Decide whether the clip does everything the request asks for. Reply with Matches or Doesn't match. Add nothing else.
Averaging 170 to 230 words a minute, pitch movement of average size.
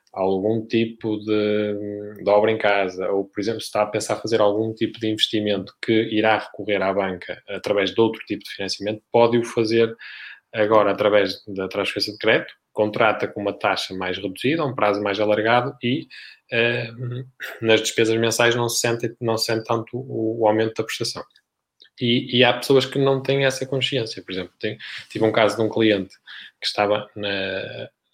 Doesn't match